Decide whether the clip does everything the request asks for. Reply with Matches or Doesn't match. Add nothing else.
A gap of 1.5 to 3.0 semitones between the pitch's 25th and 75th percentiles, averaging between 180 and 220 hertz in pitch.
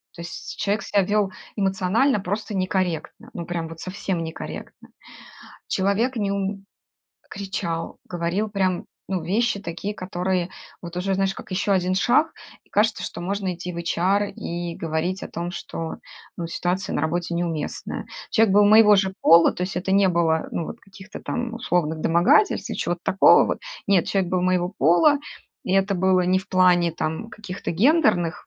Matches